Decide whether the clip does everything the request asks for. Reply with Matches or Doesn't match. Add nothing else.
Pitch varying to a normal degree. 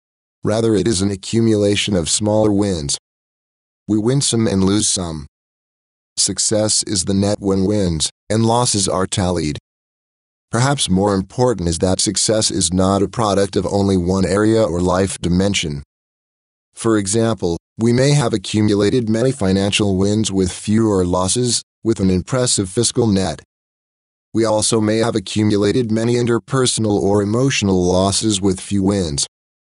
Matches